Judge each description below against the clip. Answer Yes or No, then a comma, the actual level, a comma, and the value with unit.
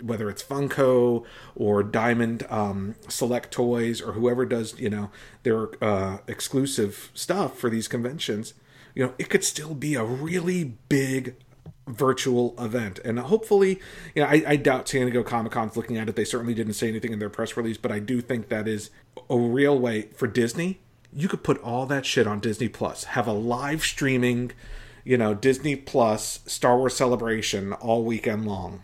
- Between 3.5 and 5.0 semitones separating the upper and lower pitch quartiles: No, average, 3.1 semitones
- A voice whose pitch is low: Yes, low, 120 Hz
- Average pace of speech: Yes, average, 185 wpm